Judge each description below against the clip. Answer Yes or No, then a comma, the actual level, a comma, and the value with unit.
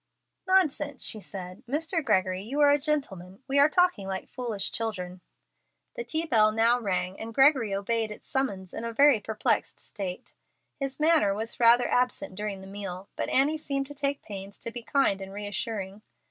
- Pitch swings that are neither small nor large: No, wide, 6.1 semitones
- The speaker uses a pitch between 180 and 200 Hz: No, high, 230 Hz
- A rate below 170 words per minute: No, average, 180 wpm